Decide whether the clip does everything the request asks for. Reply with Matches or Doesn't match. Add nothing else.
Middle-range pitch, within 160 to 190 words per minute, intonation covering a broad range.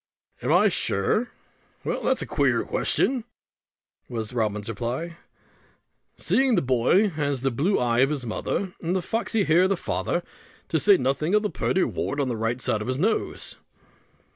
Matches